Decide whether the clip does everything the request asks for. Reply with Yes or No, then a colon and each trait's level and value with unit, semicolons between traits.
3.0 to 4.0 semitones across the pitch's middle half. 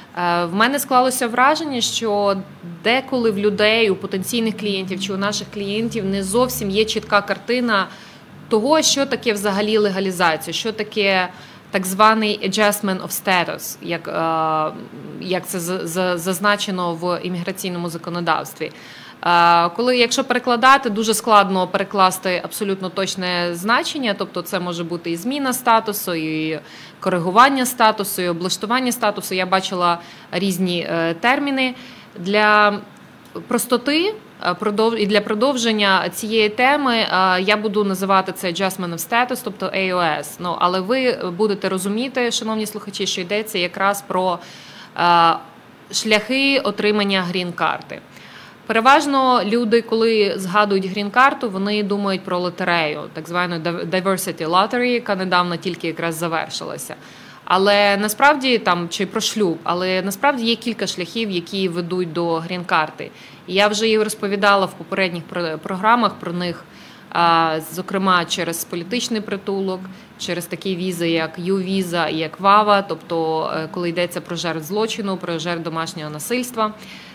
Yes: average, 3.7 semitones